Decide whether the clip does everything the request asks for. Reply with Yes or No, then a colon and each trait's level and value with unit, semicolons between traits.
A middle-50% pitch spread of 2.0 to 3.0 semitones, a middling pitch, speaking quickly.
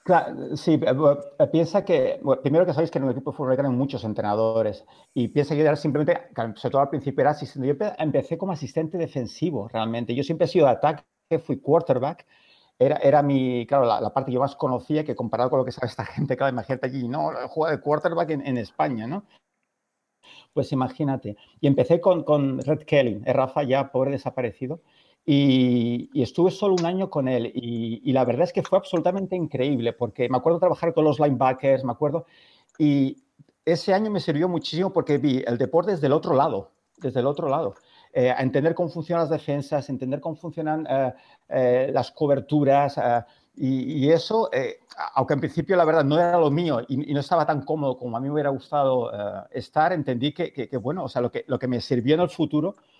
No: average, 4.1 semitones; medium, 145 Hz; fast, 210 wpm